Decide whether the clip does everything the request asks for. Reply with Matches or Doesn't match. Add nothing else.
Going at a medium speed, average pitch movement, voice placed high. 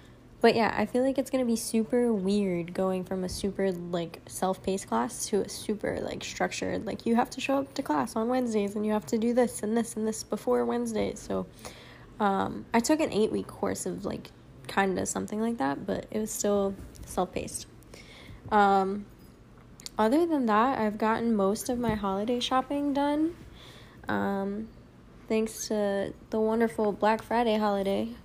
Matches